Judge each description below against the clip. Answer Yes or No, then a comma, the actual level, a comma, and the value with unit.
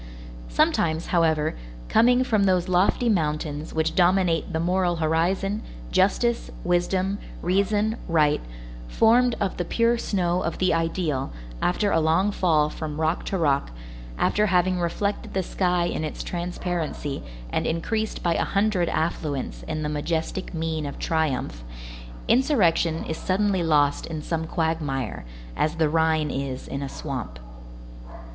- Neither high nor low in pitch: Yes, medium, 170 Hz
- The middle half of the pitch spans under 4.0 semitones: Yes, average, 3.3 semitones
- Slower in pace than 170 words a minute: Yes, average, 140 wpm